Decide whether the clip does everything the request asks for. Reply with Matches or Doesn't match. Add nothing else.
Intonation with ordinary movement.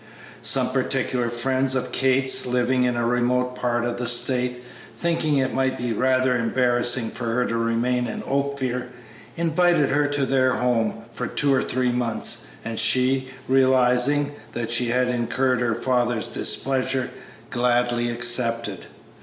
Doesn't match